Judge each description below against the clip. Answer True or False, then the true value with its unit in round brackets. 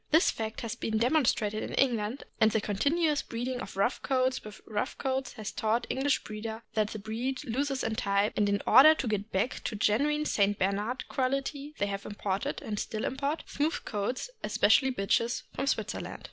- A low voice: False (230 Hz)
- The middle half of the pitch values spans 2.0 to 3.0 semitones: False (4.2 semitones)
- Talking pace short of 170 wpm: False (185 wpm)